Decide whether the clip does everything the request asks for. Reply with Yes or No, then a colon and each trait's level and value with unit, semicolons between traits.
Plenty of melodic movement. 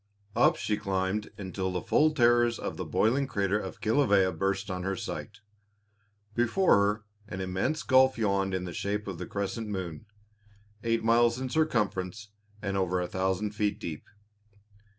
No: average, 3.6 semitones